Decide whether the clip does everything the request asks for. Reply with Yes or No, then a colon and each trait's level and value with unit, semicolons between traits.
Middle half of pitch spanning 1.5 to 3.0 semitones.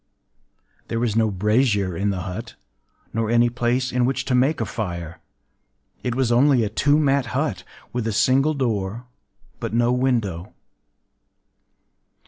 No: average, 3.8 semitones